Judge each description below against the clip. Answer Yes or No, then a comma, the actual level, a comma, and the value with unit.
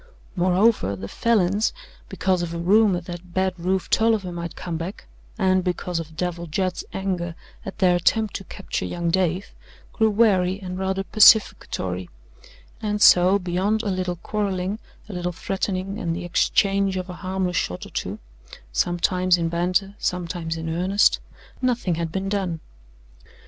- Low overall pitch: No, medium, 185 Hz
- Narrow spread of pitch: Yes, narrow, 2.1 semitones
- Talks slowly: No, average, 155 wpm